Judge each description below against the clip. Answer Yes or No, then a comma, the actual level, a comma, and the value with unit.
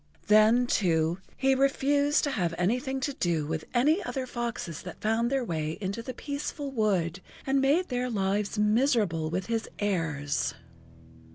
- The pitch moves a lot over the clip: Yes, wide, 7.1 semitones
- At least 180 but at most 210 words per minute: No, average, 155 wpm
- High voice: Yes, high, 225 Hz